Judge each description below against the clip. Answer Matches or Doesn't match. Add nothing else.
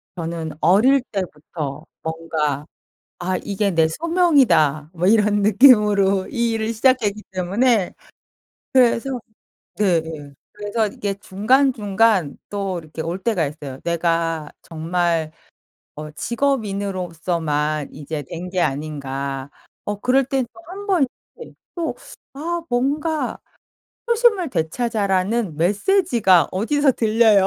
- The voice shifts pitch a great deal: Matches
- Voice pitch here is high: Matches